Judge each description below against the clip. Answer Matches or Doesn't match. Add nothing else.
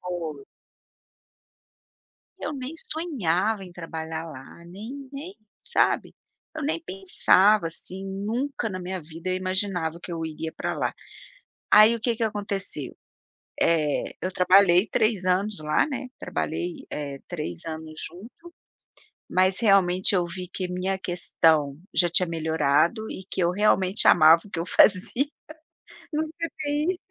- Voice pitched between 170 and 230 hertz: Matches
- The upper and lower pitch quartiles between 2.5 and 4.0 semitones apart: Doesn't match